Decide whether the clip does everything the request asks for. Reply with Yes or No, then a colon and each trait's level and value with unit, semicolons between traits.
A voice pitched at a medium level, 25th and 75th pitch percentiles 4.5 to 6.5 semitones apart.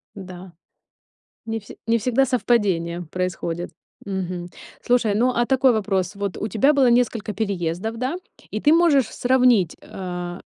No: high, 215 Hz; average, 5.1 semitones